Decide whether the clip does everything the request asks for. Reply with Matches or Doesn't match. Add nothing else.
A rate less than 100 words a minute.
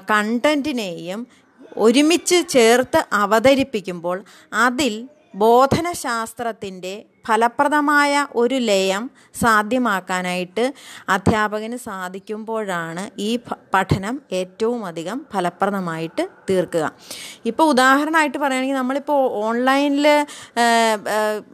Matches